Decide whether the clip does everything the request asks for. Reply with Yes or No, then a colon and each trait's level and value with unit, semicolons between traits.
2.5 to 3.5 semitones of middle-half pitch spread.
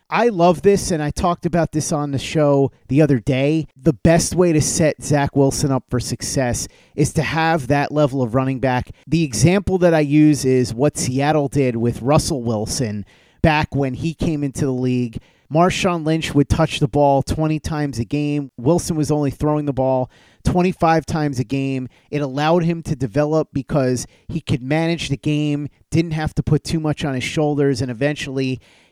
Yes: average, 3.0 semitones